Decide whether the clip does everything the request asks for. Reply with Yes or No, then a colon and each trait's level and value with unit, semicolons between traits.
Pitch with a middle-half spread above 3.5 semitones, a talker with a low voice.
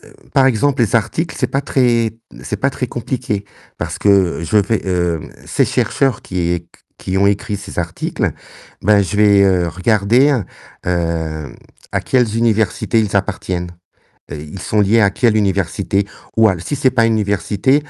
Yes: average, 3.9 semitones; low, 105 Hz